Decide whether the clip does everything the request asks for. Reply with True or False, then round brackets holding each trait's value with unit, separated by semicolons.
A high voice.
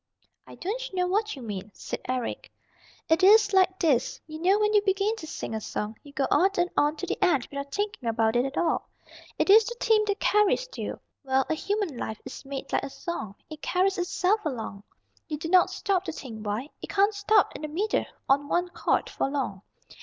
True (340 Hz)